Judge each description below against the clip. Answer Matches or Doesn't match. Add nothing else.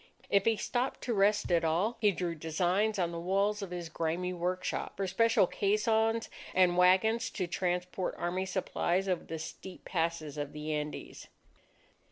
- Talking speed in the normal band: Matches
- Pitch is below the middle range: Doesn't match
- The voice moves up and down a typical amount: Matches